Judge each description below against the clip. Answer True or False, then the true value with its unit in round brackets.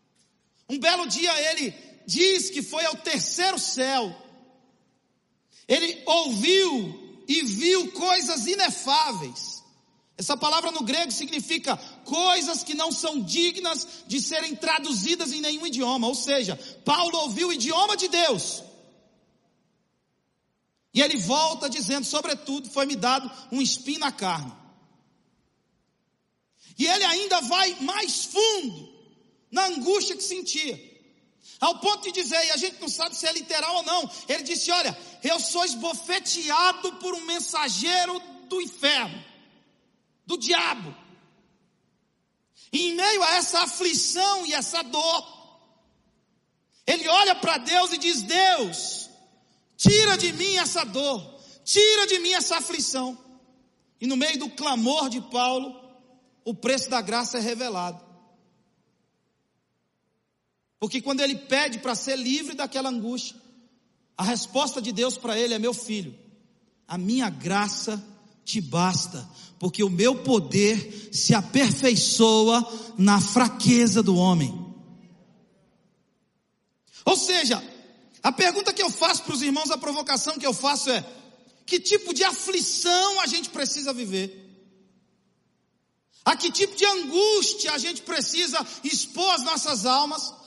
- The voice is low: False (280 Hz)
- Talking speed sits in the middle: True (130 wpm)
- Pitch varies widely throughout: True (6.1 semitones)